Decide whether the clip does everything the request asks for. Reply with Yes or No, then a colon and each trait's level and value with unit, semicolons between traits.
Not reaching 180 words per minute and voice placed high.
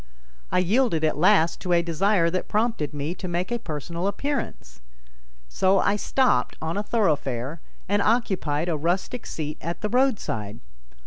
No: average, 155 wpm; medium, 175 Hz